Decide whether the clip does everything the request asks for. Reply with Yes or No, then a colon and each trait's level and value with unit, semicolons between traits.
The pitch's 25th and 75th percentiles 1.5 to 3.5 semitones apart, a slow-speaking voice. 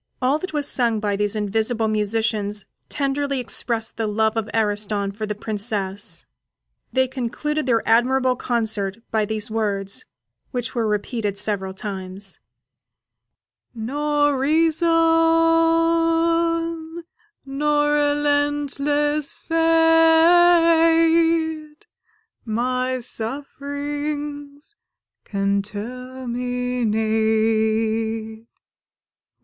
No: wide, 5.4 semitones; slow, 80 wpm